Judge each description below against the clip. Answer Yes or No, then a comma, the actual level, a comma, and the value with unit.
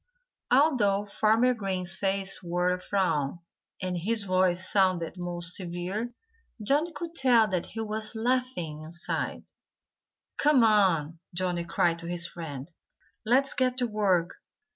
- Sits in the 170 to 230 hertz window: Yes, high, 190 Hz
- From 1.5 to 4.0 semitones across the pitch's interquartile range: No, average, 4.5 semitones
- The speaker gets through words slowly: Yes, slow, 130 wpm